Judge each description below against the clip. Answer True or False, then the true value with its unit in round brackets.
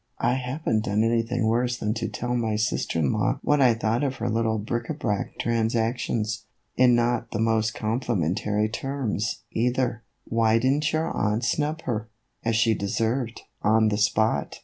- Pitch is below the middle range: True (115 Hz)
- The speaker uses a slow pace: False (180 wpm)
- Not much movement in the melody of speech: True (2.1 semitones)